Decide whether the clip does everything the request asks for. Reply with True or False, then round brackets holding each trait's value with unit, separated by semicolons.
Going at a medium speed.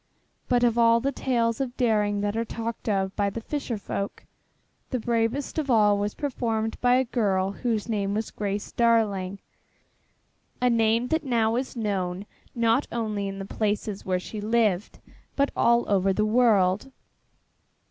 True (160 wpm)